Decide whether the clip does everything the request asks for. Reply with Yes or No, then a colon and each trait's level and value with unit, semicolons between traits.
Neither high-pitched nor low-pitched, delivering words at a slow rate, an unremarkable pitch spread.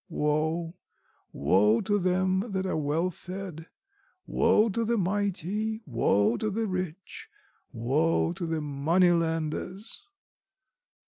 Yes: medium, 175 Hz; slow, 110 wpm; average, 4.2 semitones